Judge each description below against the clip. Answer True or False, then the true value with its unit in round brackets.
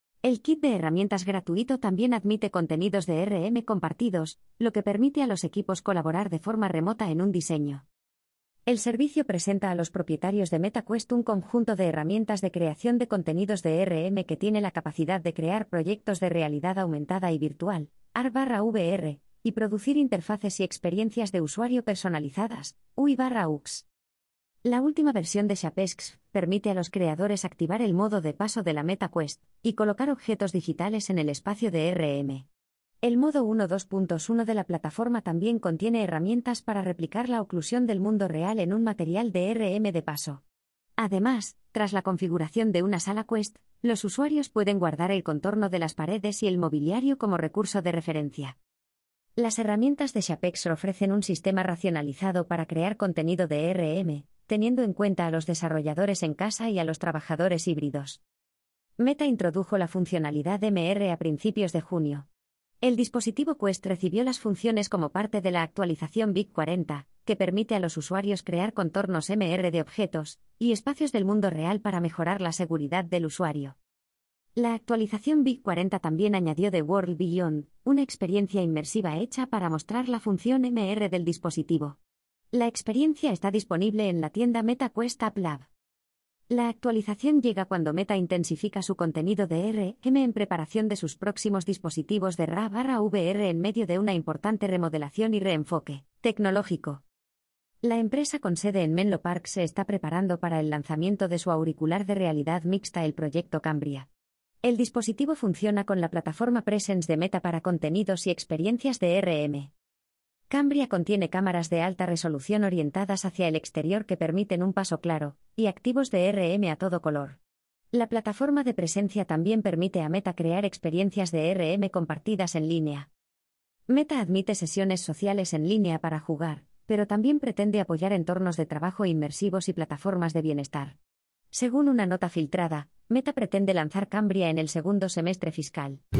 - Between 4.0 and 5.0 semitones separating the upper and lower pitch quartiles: True (4.5 semitones)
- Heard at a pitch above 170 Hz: True (190 Hz)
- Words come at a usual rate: True (165 wpm)